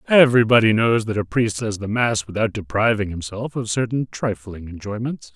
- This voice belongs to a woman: No, male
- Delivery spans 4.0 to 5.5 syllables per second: Yes, 5.3 syllables/s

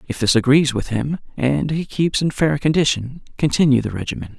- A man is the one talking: Yes, male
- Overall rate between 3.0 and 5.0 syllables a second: No, 5.4 syllables/s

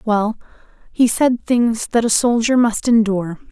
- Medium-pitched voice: No, high, 225 Hz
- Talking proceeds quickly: No, average, 155 wpm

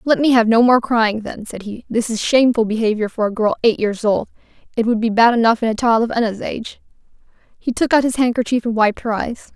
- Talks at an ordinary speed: No, fast, 245 wpm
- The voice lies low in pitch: No, high, 230 Hz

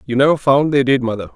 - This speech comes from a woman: No, male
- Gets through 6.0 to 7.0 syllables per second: Yes, 6.6 syllables/s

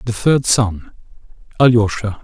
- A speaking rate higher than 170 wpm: No, slow, 105 wpm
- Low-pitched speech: Yes, low, 110 Hz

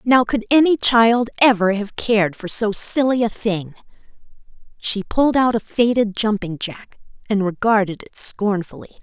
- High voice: Yes, high, 215 Hz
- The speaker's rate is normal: Yes, average, 155 wpm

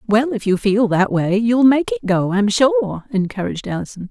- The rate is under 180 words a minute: No, fast, 205 wpm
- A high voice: Yes, high, 225 Hz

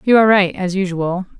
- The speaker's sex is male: No, female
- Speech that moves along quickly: Yes, fast, 215 wpm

